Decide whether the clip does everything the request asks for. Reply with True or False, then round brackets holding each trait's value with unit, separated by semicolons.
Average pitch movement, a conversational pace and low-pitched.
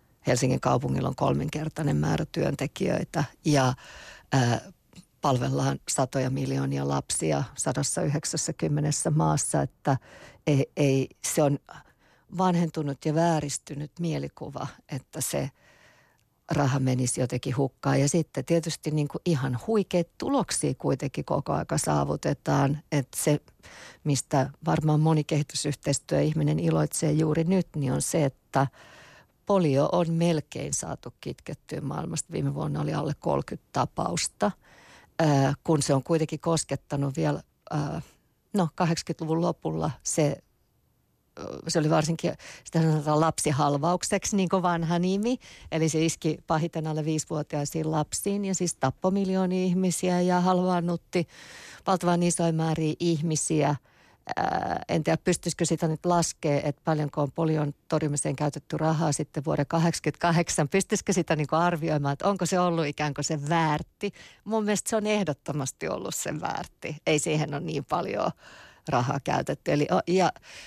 False (3.0 semitones; 130 wpm; 155 Hz)